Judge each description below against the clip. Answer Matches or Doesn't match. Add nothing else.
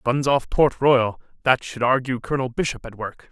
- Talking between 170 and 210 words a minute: Matches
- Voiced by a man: Matches